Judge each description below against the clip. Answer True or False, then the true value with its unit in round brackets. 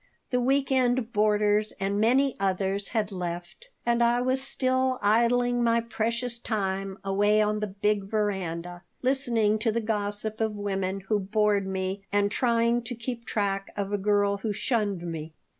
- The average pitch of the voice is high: True (210 Hz)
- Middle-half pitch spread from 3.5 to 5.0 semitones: False (3.1 semitones)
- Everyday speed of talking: True (160 wpm)